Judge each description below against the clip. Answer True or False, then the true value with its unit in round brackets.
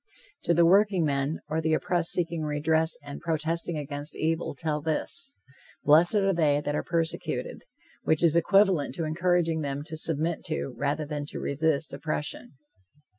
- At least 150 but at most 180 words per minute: True (155 wpm)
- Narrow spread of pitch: True (2.3 semitones)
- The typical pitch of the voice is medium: True (160 Hz)